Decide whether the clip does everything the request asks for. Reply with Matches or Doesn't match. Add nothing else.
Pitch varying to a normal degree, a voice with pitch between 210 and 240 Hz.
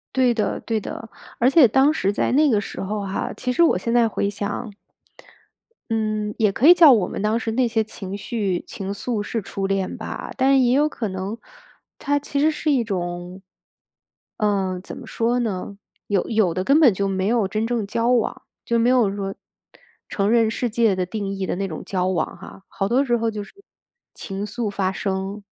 Matches